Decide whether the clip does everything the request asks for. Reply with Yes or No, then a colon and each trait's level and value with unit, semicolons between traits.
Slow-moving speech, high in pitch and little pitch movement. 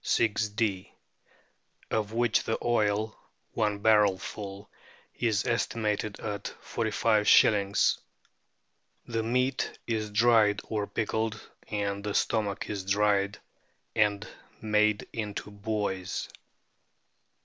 No: slow, 90 wpm; low, 105 Hz; narrow, 1.5 semitones